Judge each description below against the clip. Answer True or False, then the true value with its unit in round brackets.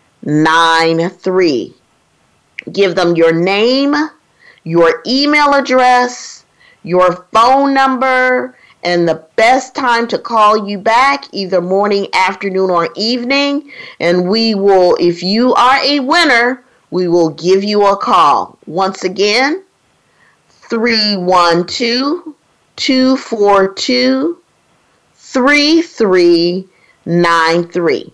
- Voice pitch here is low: False (210 Hz)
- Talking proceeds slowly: True (110 wpm)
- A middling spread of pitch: False (6.5 semitones)